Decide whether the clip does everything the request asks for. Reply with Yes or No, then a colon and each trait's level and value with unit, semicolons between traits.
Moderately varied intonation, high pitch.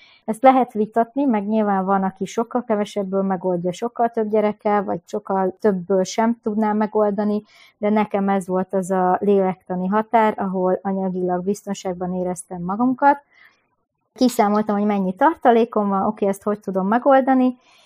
Yes: average, 3.1 semitones; high, 210 Hz